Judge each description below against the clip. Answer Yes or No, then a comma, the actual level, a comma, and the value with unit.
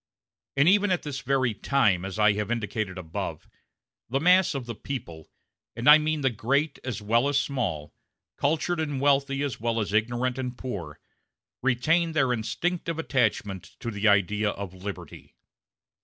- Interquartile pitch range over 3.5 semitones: Yes, average, 5.2 semitones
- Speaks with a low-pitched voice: Yes, low, 125 Hz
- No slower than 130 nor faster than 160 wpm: Yes, average, 155 wpm